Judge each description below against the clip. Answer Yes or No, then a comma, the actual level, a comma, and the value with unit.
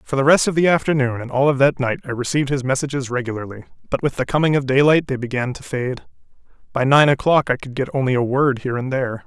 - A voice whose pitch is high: No, low, 135 Hz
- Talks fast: Yes, fast, 245 wpm